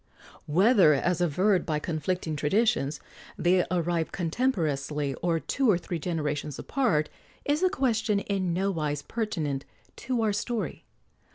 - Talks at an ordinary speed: No, slow, 125 wpm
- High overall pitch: No, medium, 175 Hz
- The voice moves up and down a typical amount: No, wide, 5.8 semitones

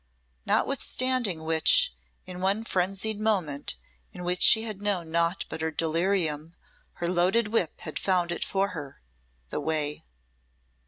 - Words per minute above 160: No, average, 140 wpm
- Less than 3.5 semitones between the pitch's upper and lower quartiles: No, average, 3.8 semitones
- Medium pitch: Yes, medium, 180 Hz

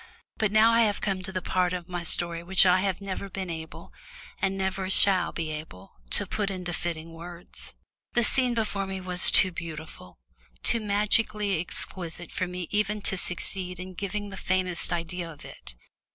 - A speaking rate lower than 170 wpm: No, average, 180 wpm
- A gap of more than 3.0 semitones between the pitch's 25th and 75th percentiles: No, narrow, 2.4 semitones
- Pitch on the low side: No, medium, 185 Hz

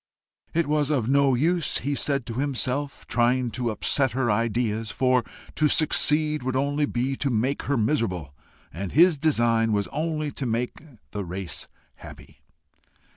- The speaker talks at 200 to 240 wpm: No, average, 150 wpm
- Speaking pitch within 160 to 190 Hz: No, low, 130 Hz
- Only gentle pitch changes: No, average, 4.1 semitones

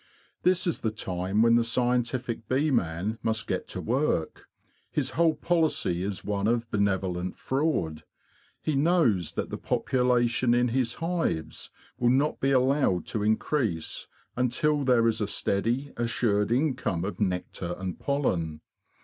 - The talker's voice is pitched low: Yes, low, 115 Hz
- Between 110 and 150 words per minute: Yes, average, 145 wpm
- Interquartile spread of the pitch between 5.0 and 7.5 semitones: Yes, average, 5.3 semitones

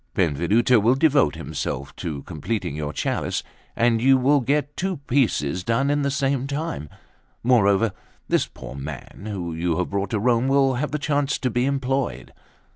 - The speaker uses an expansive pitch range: Yes, wide, 7.5 semitones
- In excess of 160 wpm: Yes, average, 170 wpm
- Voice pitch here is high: No, low, 120 Hz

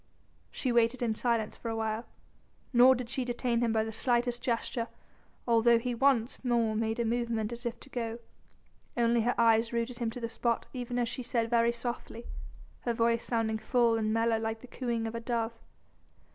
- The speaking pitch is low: No, high, 235 Hz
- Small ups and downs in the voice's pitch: Yes, narrow, 1.1 semitones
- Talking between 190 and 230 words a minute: Yes, average, 195 wpm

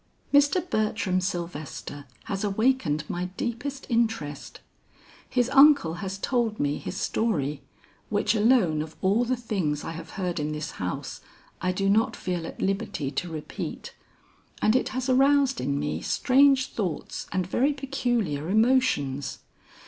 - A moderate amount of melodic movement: No, wide, 7.8 semitones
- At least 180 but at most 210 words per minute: No, average, 140 wpm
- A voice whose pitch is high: Yes, high, 200 Hz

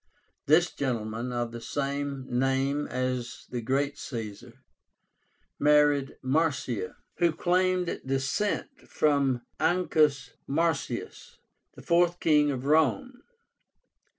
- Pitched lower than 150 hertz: Yes, medium, 140 Hz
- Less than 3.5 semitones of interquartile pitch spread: No, average, 3.8 semitones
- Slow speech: Yes, slow, 95 wpm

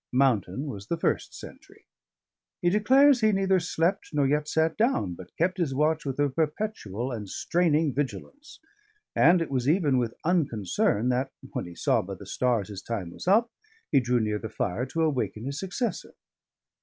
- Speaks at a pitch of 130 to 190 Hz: Yes, medium, 140 Hz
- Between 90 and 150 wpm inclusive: No, average, 180 wpm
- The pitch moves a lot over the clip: Yes, wide, 7.5 semitones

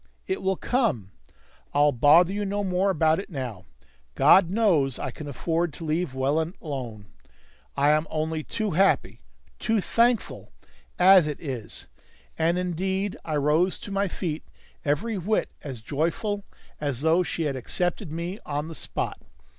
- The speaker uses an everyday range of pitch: Yes, average, 4.7 semitones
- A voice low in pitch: No, medium, 165 Hz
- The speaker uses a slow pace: No, average, 155 wpm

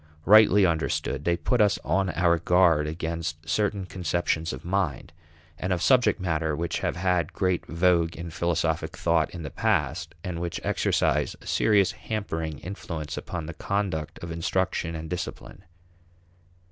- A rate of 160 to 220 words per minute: No, average, 150 wpm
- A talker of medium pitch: No, very low, 85 Hz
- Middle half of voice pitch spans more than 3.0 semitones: No, narrow, 2.5 semitones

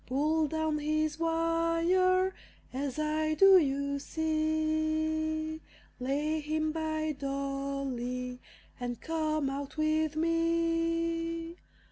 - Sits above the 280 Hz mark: Yes, very high, 315 Hz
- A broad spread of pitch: No, narrow, 2.6 semitones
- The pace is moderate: No, slow, 90 wpm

